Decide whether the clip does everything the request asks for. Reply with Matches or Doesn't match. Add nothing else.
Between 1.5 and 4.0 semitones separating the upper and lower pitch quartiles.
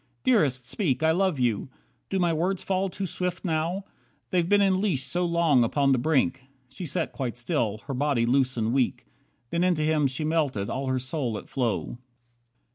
Doesn't match